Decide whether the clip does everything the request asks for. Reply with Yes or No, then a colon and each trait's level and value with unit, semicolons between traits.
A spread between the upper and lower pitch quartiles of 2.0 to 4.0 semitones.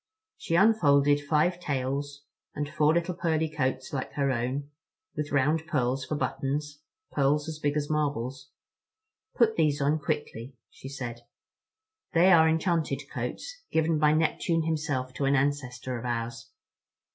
Yes: average, 3.0 semitones